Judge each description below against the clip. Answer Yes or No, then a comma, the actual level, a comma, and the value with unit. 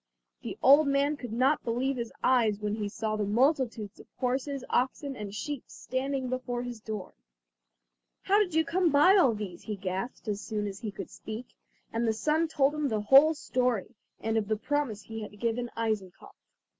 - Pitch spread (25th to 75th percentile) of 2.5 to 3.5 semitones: No, average, 4.5 semitones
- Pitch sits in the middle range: No, high, 245 Hz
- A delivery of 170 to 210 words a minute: Yes, average, 190 wpm